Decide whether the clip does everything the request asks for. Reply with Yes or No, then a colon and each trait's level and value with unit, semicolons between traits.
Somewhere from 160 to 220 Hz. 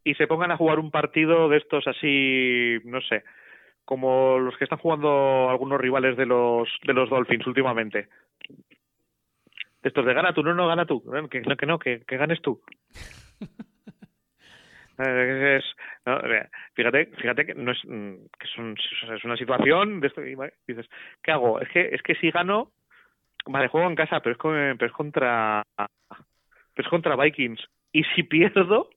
No: low, 135 Hz